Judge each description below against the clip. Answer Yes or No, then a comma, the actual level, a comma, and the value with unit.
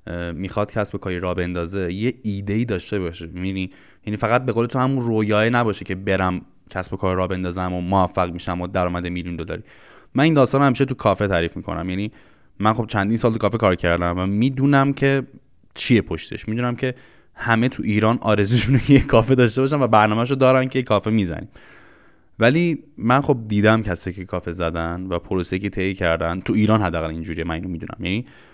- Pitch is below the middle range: Yes, low, 100 Hz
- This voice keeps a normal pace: No, fast, 185 wpm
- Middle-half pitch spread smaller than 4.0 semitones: No, average, 4.7 semitones